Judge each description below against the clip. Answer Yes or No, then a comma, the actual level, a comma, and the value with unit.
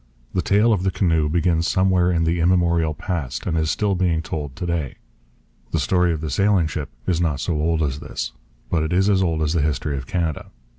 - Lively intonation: No, average, 2.7 semitones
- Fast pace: Yes, fast, 220 wpm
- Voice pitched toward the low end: Yes, very low, 85 Hz